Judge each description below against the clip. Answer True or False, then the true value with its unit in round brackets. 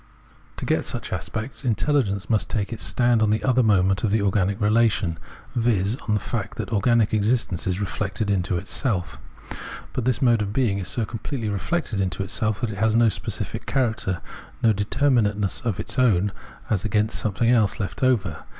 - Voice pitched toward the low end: True (110 Hz)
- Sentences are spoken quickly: False (185 wpm)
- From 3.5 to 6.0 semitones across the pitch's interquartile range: False (3.0 semitones)